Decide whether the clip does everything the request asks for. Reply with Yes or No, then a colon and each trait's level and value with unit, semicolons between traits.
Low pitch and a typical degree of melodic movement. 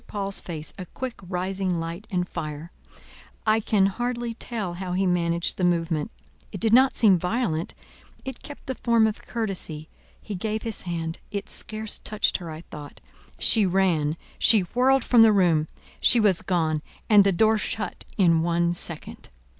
No: high, 190 Hz; average, 4.4 semitones